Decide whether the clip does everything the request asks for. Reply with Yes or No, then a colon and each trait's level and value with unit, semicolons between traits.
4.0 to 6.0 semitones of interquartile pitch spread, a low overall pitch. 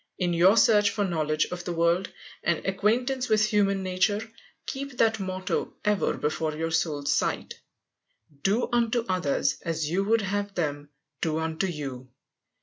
No: average, 4.5 semitones; medium, 185 Hz